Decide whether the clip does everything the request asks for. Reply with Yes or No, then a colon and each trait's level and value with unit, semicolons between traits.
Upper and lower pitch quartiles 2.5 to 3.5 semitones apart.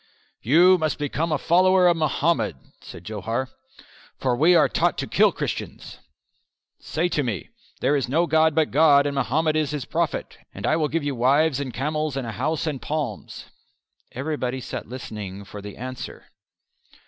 No: average, 4.1 semitones